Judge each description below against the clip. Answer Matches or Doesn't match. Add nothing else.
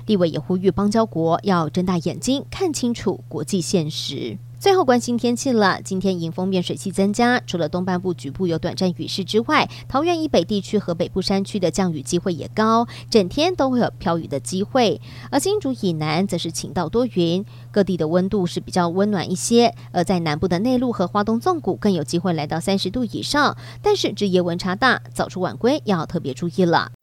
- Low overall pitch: Doesn't match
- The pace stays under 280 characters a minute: Doesn't match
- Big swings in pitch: Doesn't match